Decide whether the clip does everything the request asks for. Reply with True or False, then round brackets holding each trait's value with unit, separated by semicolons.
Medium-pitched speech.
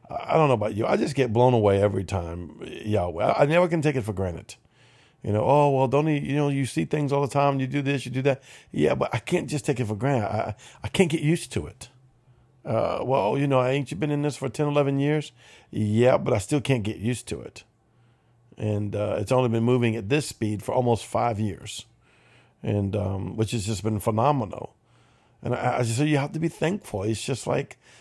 False (125 Hz)